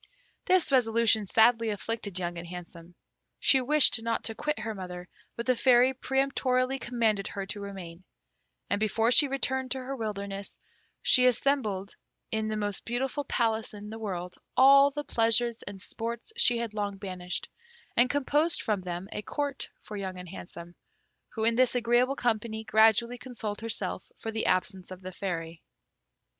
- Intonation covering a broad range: No, average, 4.2 semitones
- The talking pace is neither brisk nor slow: Yes, average, 165 wpm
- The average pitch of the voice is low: No, high, 225 Hz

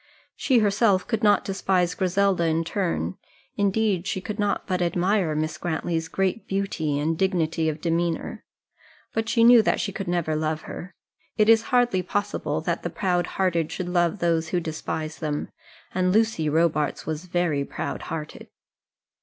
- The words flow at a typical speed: Yes, average, 160 wpm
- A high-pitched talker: No, medium, 180 Hz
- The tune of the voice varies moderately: Yes, average, 3.7 semitones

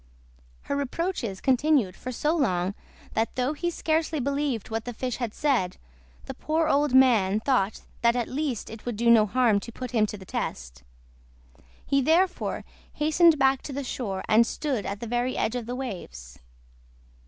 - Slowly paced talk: No, average, 175 wpm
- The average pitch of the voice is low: No, very high, 250 Hz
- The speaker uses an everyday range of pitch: Yes, average, 4.5 semitones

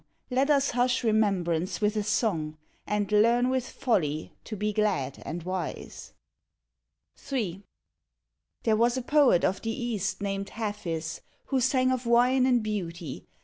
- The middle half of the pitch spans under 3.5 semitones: No, average, 4.7 semitones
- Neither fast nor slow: Yes, average, 145 wpm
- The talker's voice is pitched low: No, high, 215 Hz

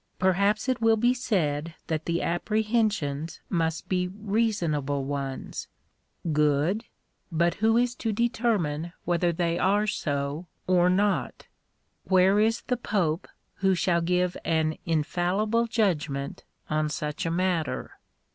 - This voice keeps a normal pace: No, slow, 125 wpm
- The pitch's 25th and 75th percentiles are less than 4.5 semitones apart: No, average, 5.2 semitones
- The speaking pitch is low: No, medium, 180 Hz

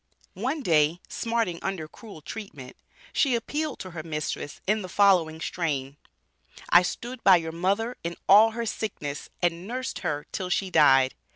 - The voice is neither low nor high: Yes, medium, 180 Hz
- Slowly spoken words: No, average, 160 wpm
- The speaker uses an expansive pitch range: Yes, wide, 5.8 semitones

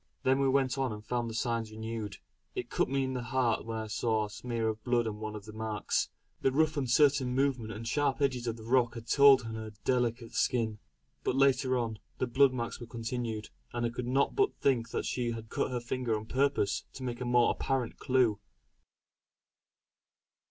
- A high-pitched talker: No, low, 120 Hz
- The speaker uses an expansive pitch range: No, average, 2.7 semitones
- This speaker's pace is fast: Yes, fast, 210 wpm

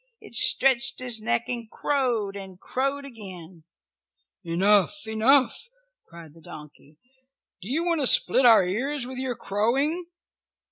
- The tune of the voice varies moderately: No, wide, 5.9 semitones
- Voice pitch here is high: Yes, high, 230 Hz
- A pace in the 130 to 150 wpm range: Yes, slow, 135 wpm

